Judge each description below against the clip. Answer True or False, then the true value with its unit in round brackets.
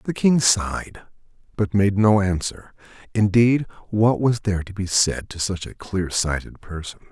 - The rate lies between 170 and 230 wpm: False (160 wpm)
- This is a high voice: False (100 Hz)